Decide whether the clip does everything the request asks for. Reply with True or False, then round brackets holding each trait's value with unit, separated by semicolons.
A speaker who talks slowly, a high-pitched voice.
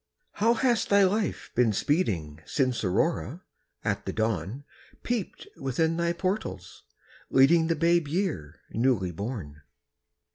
False (120 wpm; 135 Hz)